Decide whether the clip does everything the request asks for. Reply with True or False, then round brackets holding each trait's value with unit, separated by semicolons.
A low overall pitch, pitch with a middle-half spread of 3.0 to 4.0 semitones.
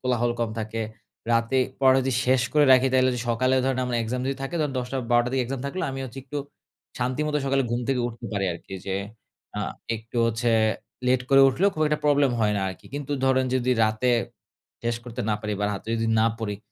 False (125 Hz; 2.6 semitones)